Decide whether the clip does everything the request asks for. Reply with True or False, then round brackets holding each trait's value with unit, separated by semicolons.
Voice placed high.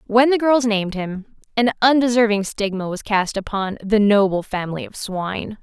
True (210 Hz)